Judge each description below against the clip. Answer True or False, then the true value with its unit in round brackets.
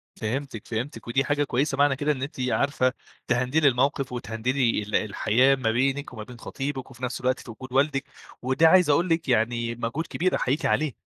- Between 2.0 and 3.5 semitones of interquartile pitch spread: True (3.1 semitones)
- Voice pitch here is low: True (130 Hz)